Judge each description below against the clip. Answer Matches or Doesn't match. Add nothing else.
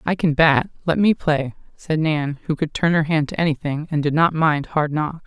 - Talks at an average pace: Doesn't match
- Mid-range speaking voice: Matches